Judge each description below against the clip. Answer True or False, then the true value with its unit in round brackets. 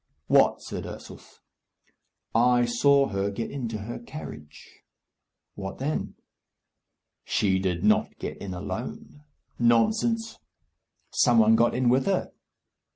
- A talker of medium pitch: False (120 Hz)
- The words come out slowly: True (115 wpm)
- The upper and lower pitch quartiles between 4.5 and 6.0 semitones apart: True (5.1 semitones)